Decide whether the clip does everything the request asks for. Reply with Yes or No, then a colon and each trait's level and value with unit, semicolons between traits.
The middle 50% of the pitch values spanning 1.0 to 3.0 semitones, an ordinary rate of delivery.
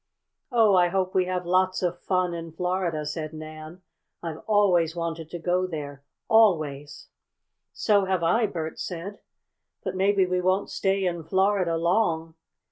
Yes: narrow, 2.6 semitones; average, 150 wpm